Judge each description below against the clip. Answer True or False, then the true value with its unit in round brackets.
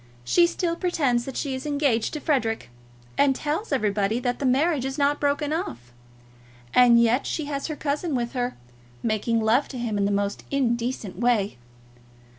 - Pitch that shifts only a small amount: False (4.2 semitones)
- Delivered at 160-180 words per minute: True (175 wpm)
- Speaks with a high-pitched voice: True (255 Hz)